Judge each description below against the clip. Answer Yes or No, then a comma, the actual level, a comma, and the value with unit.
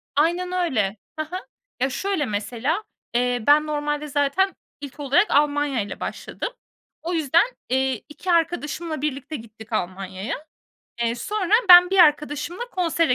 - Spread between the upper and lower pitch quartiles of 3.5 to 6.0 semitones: Yes, average, 5.1 semitones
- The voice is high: Yes, very high, 295 Hz